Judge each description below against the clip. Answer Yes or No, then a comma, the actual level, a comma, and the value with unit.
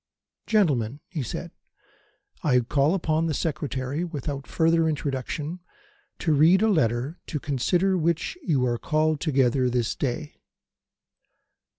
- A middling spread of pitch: Yes, average, 4.0 semitones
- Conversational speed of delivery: No, slow, 120 wpm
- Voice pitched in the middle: Yes, medium, 150 Hz